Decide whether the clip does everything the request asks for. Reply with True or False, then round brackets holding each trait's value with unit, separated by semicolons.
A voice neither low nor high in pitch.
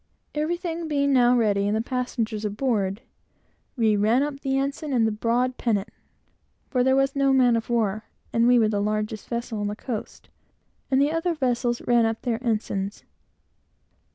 False (240 Hz)